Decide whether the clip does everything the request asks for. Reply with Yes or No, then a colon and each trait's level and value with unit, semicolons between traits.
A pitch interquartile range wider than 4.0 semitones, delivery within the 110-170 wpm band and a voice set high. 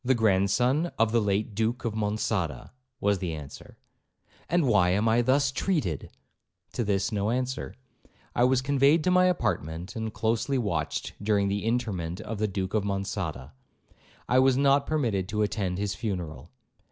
No: average, 4.5 semitones; average, 165 wpm; low, 110 Hz